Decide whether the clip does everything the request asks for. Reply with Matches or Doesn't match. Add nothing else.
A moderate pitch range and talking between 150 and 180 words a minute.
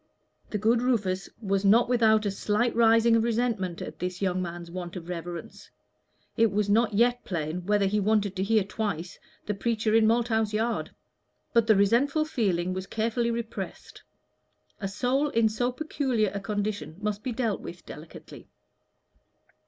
Matches